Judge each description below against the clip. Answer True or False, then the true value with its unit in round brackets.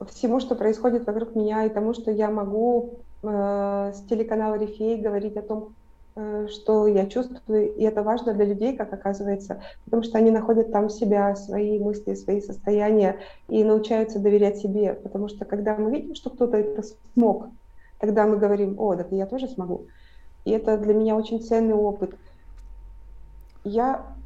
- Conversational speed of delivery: False (165 wpm)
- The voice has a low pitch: False (215 Hz)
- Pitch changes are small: True (1.5 semitones)